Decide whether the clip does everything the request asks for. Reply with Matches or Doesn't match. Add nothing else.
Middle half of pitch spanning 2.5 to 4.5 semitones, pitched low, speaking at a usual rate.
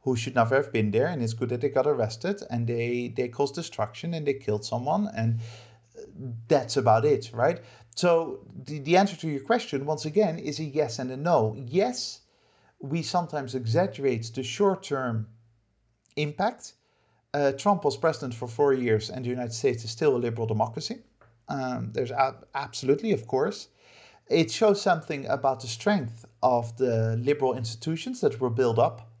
Doesn't match